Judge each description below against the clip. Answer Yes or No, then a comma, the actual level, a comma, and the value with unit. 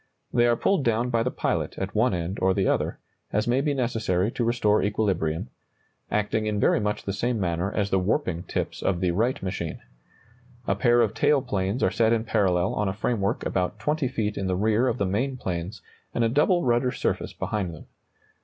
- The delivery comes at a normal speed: No, fast, 210 wpm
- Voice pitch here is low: Yes, low, 105 Hz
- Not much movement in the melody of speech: No, average, 4.1 semitones